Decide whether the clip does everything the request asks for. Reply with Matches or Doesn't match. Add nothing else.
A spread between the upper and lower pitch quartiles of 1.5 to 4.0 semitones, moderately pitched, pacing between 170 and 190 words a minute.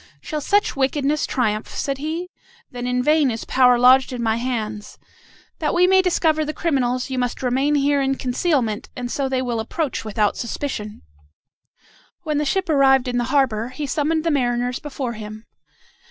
Doesn't match